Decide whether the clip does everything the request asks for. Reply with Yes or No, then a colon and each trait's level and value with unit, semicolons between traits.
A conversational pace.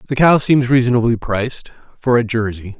Yes: average, 170 wpm